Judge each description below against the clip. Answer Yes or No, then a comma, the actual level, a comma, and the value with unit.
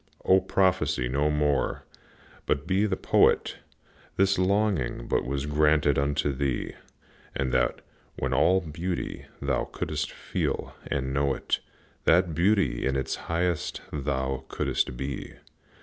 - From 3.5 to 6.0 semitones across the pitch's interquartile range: Yes, average, 4.8 semitones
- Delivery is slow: Yes, slow, 125 wpm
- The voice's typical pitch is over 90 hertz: No, very low, 75 Hz